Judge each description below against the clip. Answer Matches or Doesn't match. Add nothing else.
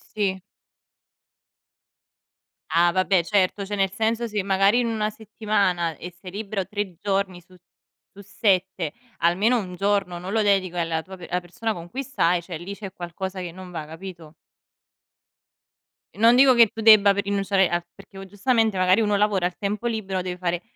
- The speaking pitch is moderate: Doesn't match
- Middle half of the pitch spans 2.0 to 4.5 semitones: Matches